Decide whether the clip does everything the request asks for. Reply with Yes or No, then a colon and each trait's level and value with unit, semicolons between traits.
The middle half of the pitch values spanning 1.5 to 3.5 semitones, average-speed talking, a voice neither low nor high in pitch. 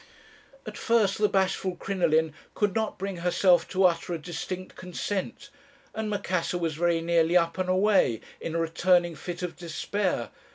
Yes: narrow, 2.6 semitones; average, 160 wpm; medium, 180 Hz